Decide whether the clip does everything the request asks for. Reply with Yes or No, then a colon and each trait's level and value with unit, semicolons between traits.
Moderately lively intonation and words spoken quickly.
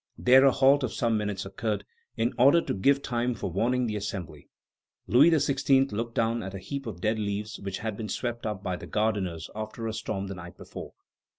Yes: average, 4.0 semitones; fast, 210 wpm